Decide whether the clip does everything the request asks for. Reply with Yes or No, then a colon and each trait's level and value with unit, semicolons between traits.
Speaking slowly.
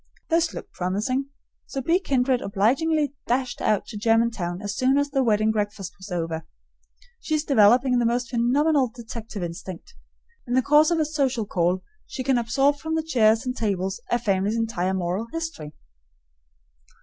No: average, 165 wpm